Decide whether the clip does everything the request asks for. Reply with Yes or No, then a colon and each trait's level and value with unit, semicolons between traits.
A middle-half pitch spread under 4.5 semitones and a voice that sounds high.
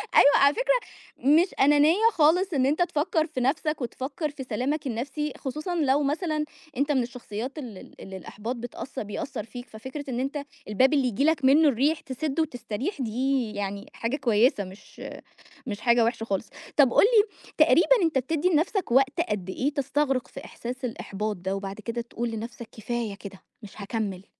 No: average, 4.8 semitones; very high, 260 Hz